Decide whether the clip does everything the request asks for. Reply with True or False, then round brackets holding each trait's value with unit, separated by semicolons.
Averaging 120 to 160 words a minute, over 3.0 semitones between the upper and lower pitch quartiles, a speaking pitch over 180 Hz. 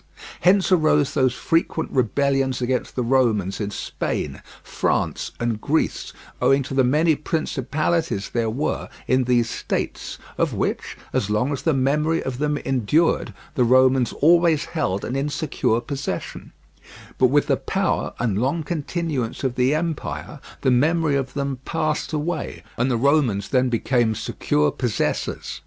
False (145 wpm; 3.8 semitones; 135 Hz)